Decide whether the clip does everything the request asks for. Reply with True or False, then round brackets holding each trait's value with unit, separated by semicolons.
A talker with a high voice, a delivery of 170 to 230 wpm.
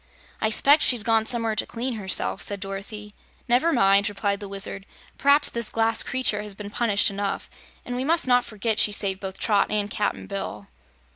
True (210 Hz; 190 wpm)